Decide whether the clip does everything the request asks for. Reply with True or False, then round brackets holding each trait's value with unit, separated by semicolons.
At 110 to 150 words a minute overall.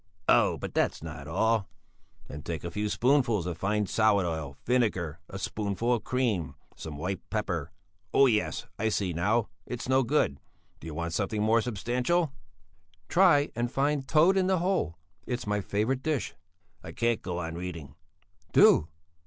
False (165 wpm)